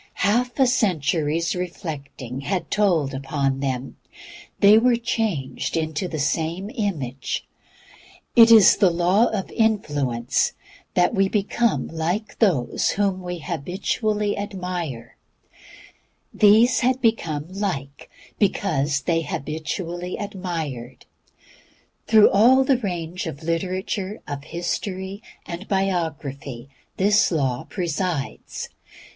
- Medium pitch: Yes, medium, 180 Hz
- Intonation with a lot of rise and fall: Yes, wide, 5.7 semitones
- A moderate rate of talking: No, slow, 105 wpm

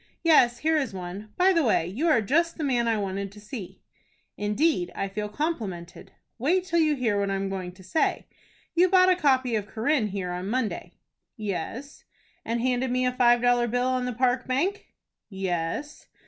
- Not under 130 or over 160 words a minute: No, average, 190 wpm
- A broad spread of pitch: Yes, wide, 6.4 semitones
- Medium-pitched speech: No, high, 240 Hz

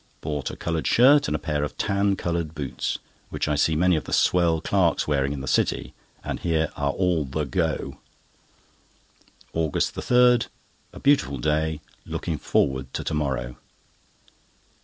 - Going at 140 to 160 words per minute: Yes, average, 155 wpm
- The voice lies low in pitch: Yes, very low, 80 Hz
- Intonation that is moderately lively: Yes, average, 3.7 semitones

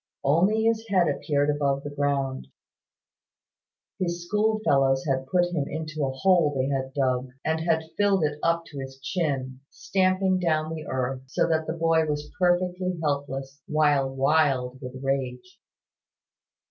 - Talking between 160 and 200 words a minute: No, average, 145 wpm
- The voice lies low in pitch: No, medium, 150 Hz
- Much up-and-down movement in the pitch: No, average, 4.4 semitones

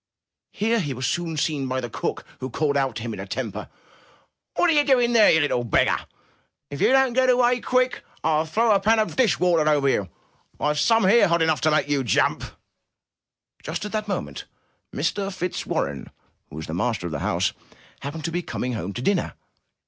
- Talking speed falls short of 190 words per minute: No, fast, 205 wpm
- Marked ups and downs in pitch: Yes, wide, 8.9 semitones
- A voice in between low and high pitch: Yes, medium, 160 Hz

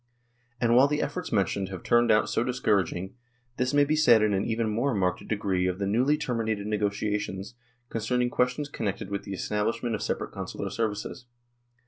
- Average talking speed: Yes, average, 185 wpm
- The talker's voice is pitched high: No, low, 115 Hz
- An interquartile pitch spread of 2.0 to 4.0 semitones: Yes, average, 3.5 semitones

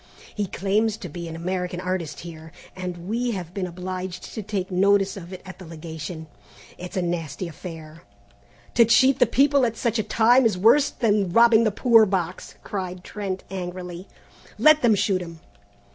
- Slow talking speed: No, average, 175 wpm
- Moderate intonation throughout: Yes, average, 3.8 semitones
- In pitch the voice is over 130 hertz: Yes, medium, 185 Hz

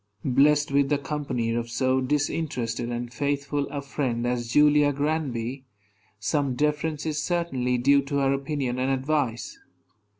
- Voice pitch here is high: No, medium, 140 Hz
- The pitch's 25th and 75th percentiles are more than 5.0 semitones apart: No, average, 3.1 semitones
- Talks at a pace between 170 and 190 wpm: No, average, 140 wpm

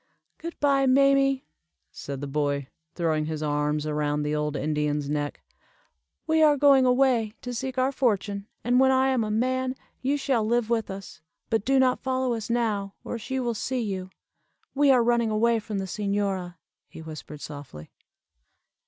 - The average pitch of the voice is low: No, high, 225 Hz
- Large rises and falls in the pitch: Yes, wide, 8.9 semitones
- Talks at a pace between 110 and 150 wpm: No, average, 170 wpm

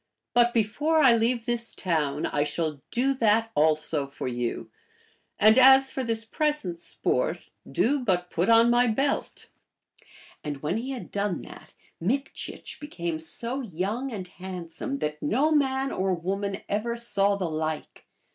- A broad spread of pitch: Yes, wide, 6.7 semitones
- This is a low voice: No, high, 215 Hz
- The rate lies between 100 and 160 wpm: Yes, average, 150 wpm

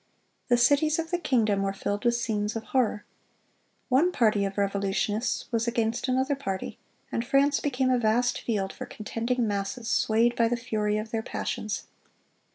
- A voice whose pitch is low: No, high, 230 Hz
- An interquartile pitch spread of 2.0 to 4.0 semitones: Yes, average, 3.3 semitones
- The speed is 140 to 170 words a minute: Yes, average, 165 wpm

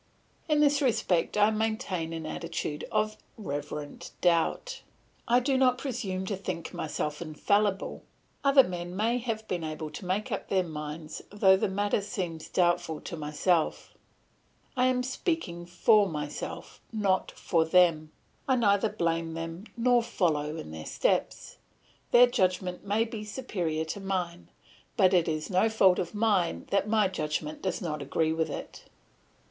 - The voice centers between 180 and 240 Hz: Yes, medium, 185 Hz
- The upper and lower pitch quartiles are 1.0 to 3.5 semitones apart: No, average, 5.0 semitones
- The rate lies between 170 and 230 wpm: No, average, 155 wpm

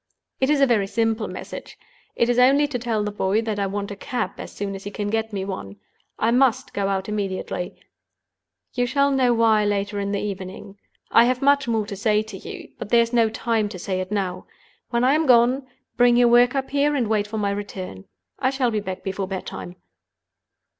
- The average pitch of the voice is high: Yes, high, 220 Hz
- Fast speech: Yes, fast, 220 wpm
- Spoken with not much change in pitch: No, average, 3.5 semitones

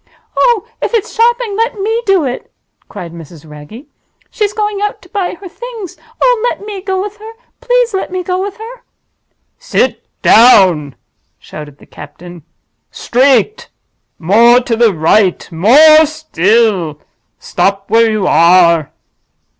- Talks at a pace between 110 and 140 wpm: Yes, slow, 135 wpm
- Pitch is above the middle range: Yes, very high, 290 Hz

